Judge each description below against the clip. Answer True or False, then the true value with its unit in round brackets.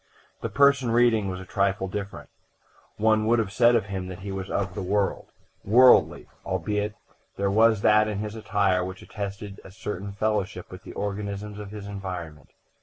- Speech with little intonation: True (1.8 semitones)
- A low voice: True (100 Hz)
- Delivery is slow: False (180 wpm)